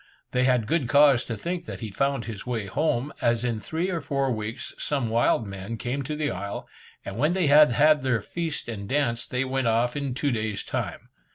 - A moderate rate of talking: No, fast, 215 wpm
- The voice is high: No, low, 125 Hz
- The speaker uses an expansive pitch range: No, average, 4.2 semitones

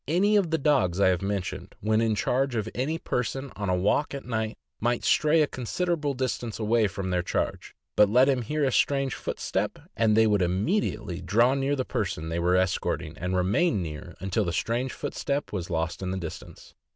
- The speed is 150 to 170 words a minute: No, average, 200 wpm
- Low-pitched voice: Yes, low, 110 Hz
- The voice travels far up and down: Yes, wide, 6.6 semitones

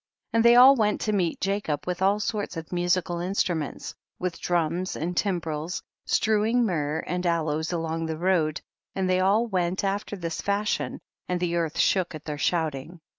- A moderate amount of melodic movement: Yes, average, 3.4 semitones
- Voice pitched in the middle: Yes, medium, 180 Hz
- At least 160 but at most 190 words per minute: Yes, average, 185 wpm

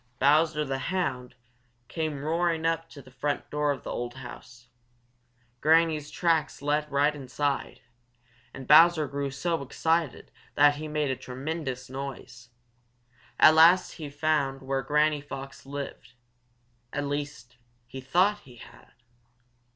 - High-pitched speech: No, medium, 145 Hz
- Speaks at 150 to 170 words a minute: No, slow, 135 wpm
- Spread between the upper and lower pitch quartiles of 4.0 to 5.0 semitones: No, average, 2.8 semitones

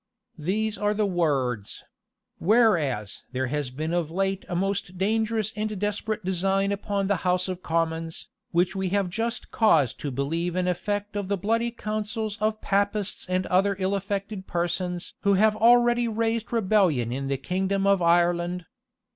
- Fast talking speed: No, average, 165 wpm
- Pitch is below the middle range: No, high, 195 Hz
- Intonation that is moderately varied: Yes, average, 3.5 semitones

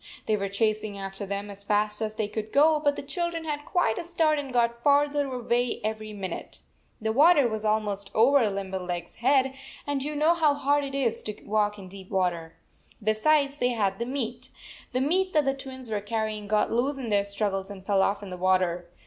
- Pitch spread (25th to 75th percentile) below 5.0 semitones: No, wide, 5.6 semitones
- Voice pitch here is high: Yes, high, 220 Hz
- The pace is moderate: No, fast, 225 wpm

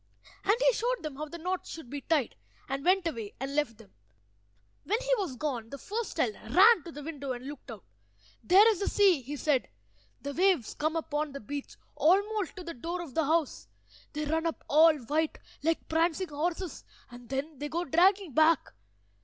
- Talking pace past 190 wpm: Yes, average, 200 wpm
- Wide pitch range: No, average, 4.3 semitones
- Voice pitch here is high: Yes, very high, 315 Hz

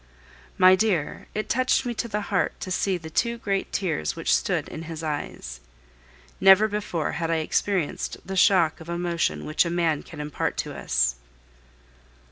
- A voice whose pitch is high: No, medium, 175 Hz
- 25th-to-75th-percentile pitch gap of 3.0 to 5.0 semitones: Yes, average, 4.1 semitones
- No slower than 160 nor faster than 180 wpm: Yes, average, 170 wpm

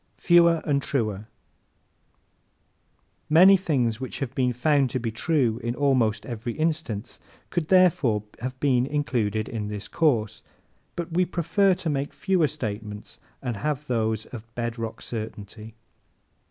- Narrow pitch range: No, wide, 5.6 semitones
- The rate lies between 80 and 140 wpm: Yes, slow, 135 wpm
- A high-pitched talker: No, low, 125 Hz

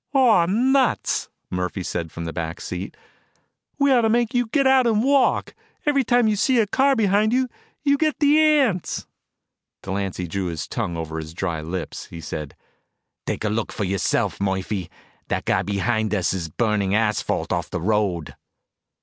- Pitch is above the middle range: No, low, 110 Hz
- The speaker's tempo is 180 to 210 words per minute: No, average, 165 wpm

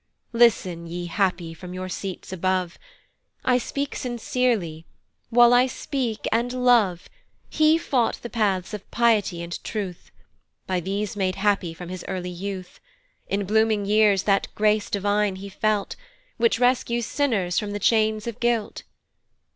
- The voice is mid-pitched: No, high, 205 Hz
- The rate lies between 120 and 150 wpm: Yes, average, 145 wpm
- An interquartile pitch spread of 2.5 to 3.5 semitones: No, average, 4.1 semitones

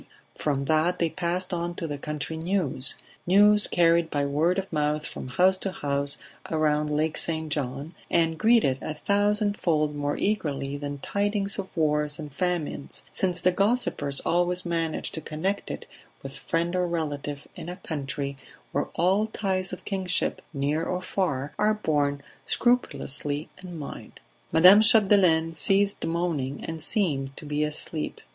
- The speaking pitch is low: No, medium, 165 Hz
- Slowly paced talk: No, average, 150 wpm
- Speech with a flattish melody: No, average, 4.0 semitones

